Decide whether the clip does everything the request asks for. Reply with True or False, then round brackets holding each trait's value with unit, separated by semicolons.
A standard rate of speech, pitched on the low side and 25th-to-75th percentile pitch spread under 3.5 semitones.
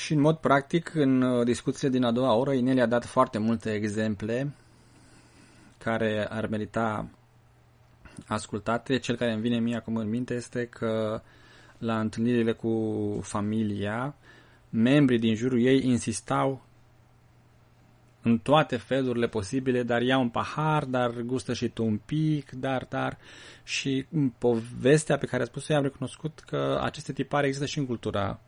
True (150 wpm; 120 Hz; 2.9 semitones)